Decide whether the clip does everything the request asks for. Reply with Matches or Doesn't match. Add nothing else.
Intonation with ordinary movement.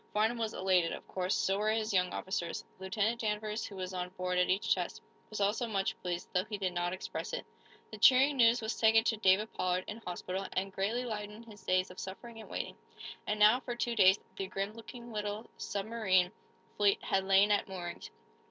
Matches